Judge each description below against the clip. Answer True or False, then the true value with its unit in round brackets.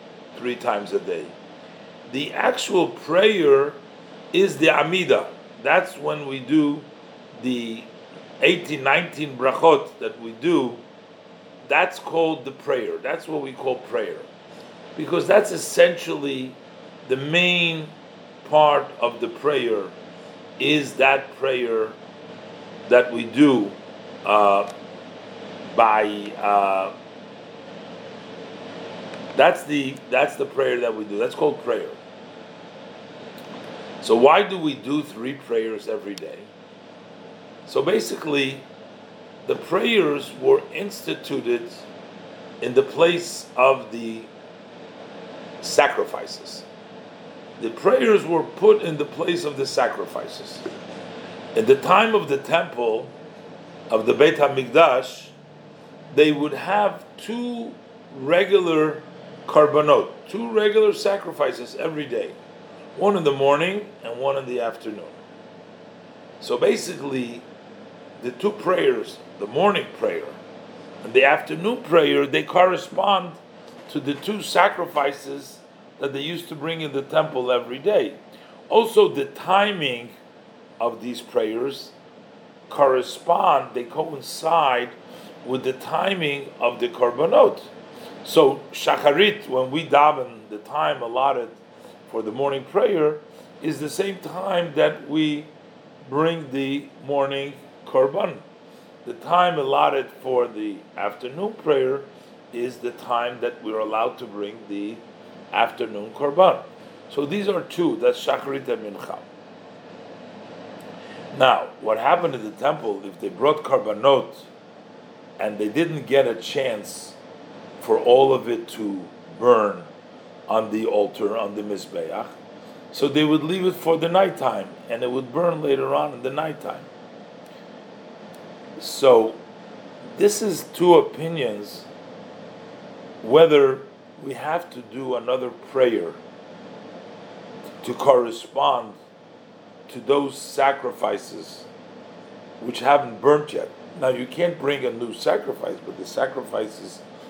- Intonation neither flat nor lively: False (8.0 semitones)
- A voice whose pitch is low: False (150 Hz)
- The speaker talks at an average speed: False (120 wpm)